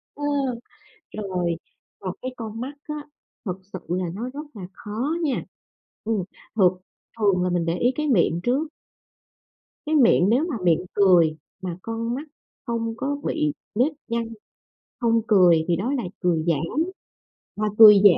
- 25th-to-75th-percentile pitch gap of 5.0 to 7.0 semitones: Yes, wide, 5.5 semitones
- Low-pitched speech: No, high, 215 Hz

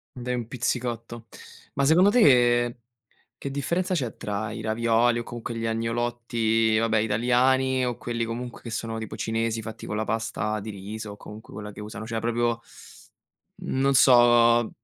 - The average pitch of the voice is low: Yes, low, 115 Hz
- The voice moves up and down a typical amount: No, narrow, 1.7 semitones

